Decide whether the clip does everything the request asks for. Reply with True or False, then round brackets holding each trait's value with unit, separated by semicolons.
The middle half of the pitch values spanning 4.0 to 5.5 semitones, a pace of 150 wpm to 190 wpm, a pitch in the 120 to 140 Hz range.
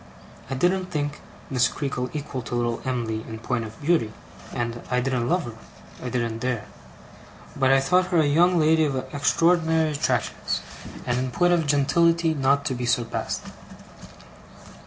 True (4.8 semitones; 160 wpm; 135 Hz)